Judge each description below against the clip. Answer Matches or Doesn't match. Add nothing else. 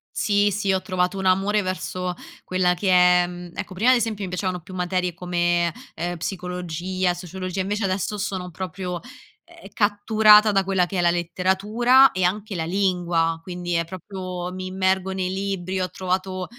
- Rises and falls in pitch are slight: Matches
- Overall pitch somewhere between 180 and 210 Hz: Matches